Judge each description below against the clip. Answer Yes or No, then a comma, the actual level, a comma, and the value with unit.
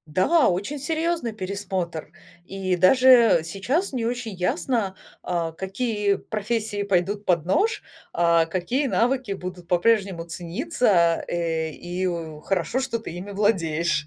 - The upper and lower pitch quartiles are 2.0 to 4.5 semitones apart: No, average, 5.0 semitones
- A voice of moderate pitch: No, high, 195 Hz